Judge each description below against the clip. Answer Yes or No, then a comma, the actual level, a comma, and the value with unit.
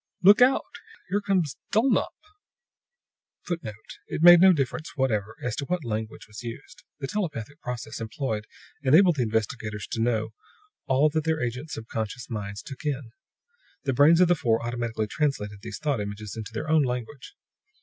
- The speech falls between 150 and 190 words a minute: Yes, average, 160 wpm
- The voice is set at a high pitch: No, low, 125 Hz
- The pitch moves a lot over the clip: Yes, wide, 6.0 semitones